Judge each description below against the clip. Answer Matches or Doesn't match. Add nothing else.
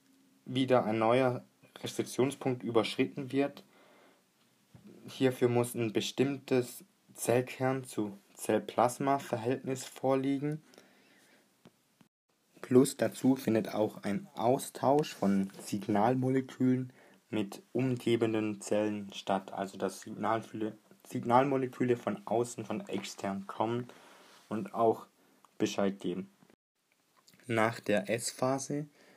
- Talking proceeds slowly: Matches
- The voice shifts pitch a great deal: Doesn't match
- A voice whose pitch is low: Matches